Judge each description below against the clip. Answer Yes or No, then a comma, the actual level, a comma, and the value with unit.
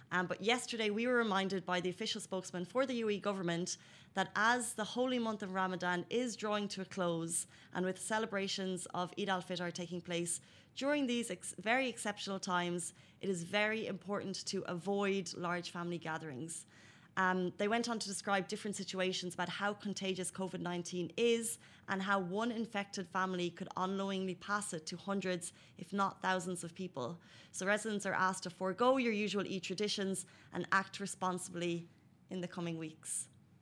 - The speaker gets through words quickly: Yes, fast, 175 wpm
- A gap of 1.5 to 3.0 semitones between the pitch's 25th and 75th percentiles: Yes, narrow, 2.5 semitones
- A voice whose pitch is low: No, high, 190 Hz